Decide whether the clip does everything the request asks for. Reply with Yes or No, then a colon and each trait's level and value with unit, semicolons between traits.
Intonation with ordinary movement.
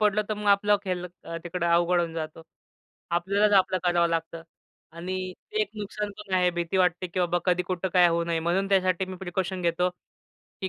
No: narrow, 2.1 semitones